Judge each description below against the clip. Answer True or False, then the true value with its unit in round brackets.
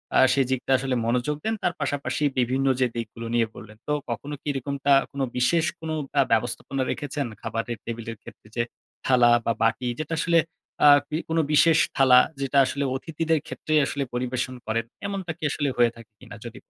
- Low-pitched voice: True (130 Hz)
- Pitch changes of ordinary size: True (3.8 semitones)